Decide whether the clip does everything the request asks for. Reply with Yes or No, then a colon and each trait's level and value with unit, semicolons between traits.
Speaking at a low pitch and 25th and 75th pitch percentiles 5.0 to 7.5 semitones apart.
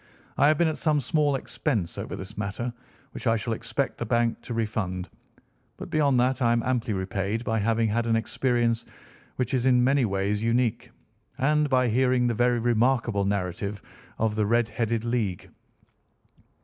No: low, 115 Hz; average, 2.9 semitones